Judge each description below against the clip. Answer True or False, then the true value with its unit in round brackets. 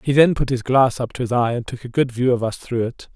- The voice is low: True (125 Hz)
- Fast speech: True (340 wpm)